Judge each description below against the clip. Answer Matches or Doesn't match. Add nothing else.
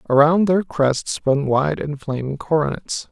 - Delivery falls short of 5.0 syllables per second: Matches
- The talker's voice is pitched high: Doesn't match